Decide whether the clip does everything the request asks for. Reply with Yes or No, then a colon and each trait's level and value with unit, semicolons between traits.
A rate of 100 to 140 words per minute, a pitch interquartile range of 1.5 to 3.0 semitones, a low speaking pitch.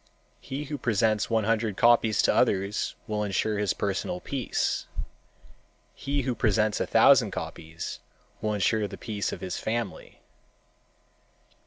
Yes: slow, 135 wpm; average, 2.7 semitones; low, 110 Hz